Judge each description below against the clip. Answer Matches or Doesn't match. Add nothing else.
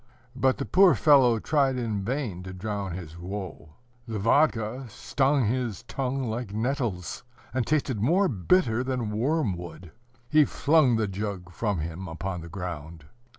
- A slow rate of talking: Doesn't match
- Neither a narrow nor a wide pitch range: Doesn't match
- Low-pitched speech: Matches